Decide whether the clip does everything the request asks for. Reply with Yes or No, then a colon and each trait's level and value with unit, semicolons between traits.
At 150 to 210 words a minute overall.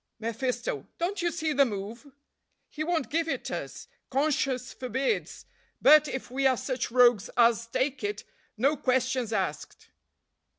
No: average, 140 wpm